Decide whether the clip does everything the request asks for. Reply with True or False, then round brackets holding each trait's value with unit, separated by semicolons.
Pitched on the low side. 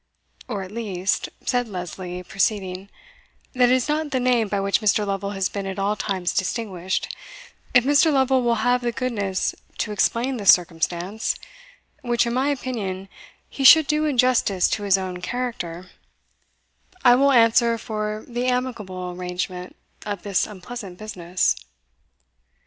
False (210 Hz)